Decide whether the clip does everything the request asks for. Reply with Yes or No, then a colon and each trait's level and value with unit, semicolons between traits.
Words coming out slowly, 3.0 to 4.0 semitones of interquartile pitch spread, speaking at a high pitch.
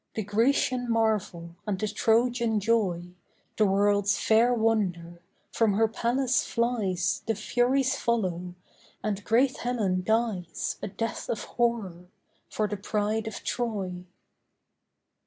Yes: slow, 120 wpm; average, 3.4 semitones; high, 215 Hz